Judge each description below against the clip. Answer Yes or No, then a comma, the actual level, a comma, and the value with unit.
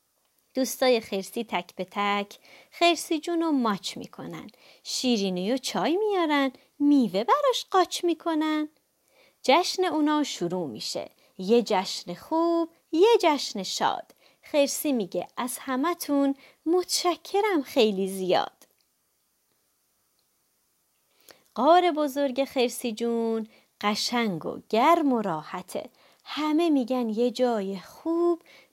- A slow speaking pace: Yes, slow, 100 wpm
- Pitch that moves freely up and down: Yes, wide, 6.8 semitones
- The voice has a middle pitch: No, very high, 270 Hz